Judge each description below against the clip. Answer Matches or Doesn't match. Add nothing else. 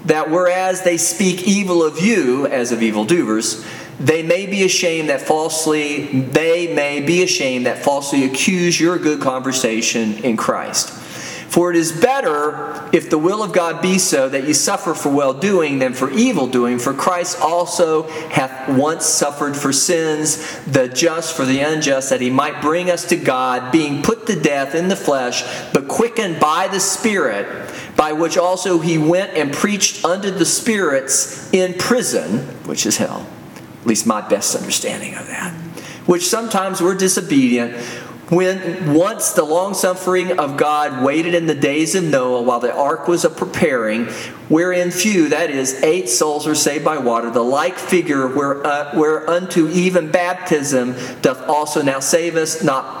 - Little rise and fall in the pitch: Doesn't match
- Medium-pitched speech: Matches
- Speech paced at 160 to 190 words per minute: Matches